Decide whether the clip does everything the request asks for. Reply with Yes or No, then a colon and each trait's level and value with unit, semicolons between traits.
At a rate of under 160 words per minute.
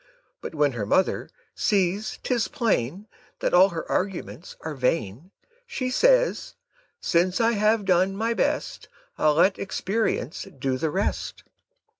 Yes: slow, 135 wpm